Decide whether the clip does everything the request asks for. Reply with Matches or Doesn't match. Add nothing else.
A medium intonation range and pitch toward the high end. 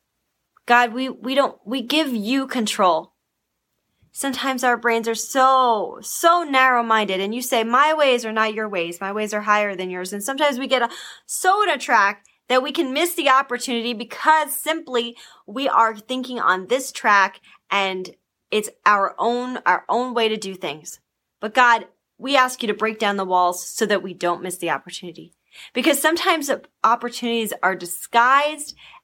Matches